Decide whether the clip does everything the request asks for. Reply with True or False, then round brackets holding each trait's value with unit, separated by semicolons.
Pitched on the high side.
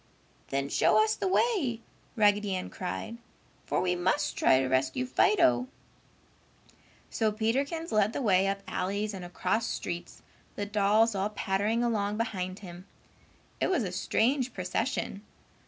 True (205 Hz)